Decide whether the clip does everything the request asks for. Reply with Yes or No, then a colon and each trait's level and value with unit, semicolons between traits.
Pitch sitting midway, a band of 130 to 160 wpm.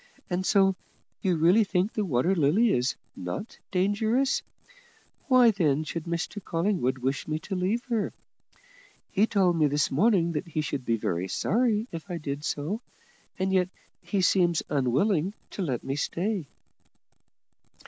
Yes: medium, 180 Hz; average, 150 wpm